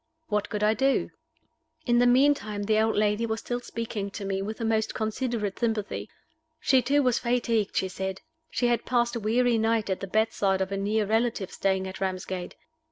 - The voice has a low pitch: No, high, 220 Hz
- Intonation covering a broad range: No, average, 3.2 semitones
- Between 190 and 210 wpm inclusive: Yes, average, 195 wpm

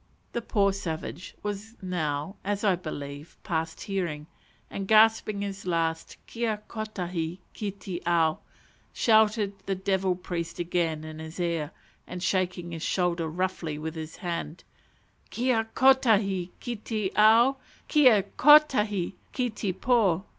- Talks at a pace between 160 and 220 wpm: No, slow, 135 wpm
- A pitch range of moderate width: Yes, average, 4.2 semitones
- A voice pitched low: No, high, 190 Hz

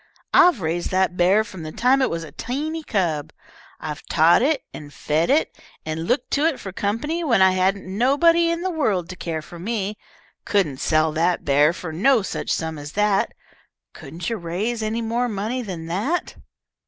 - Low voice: No, high, 195 Hz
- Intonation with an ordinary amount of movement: No, wide, 6.9 semitones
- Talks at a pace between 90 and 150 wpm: No, average, 190 wpm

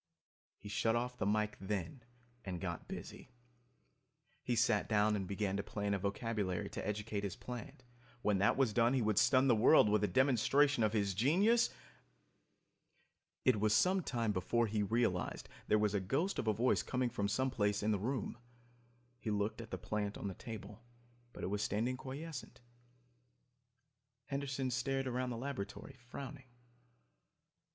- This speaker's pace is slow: No, average, 165 wpm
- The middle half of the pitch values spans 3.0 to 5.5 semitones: Yes, average, 3.8 semitones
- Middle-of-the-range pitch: No, low, 110 Hz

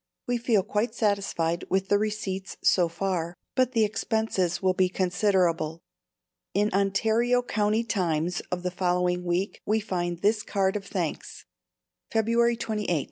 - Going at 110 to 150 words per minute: Yes, average, 140 wpm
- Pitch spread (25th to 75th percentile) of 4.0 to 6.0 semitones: No, average, 3.5 semitones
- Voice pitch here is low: No, high, 195 Hz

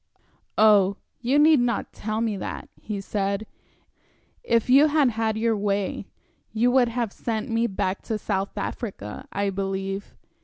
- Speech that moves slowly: No, average, 150 wpm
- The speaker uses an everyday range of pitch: Yes, average, 3.0 semitones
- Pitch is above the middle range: Yes, high, 215 Hz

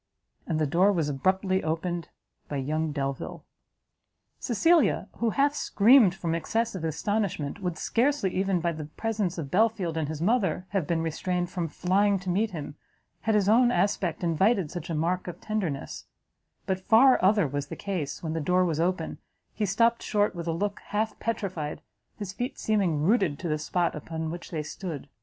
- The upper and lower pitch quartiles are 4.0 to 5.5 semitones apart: Yes, average, 4.3 semitones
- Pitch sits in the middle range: Yes, medium, 180 Hz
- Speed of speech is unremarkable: Yes, average, 180 wpm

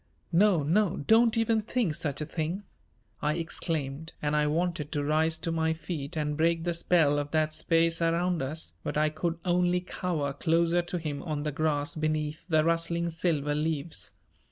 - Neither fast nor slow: Yes, average, 180 wpm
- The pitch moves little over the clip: Yes, narrow, 2.2 semitones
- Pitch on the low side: No, medium, 160 Hz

